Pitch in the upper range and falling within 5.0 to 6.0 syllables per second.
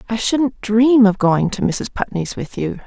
No: high, 215 Hz; 4.2 syllables/s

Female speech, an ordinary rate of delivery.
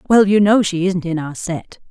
No: female; fast, 250 wpm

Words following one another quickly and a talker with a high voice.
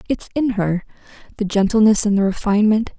No: average, 140 wpm; high, 210 Hz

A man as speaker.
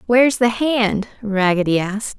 No: female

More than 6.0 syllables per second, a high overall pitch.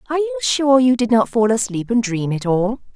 No: 5.6 syllables/s; high, 240 Hz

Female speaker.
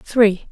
Yes: female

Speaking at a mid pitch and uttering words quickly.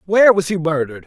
Yes: medium, 175 Hz; fast, 225 wpm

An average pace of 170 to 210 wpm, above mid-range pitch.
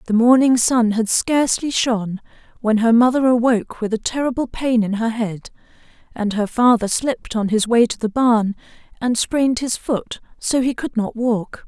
Yes: average, 185 wpm; high, 235 Hz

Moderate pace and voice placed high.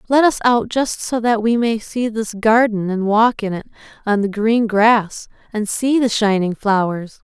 Yes: average, 195 wpm; high, 220 Hz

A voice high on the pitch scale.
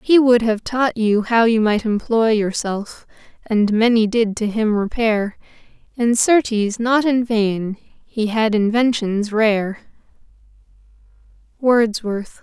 Yes: high, 225 Hz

